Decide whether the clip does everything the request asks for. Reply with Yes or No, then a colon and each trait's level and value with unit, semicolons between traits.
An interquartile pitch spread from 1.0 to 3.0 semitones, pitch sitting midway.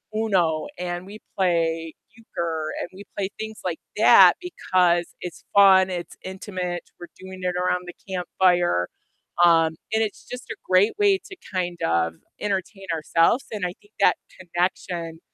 Yes: narrow, 2.4 semitones; medium, 180 Hz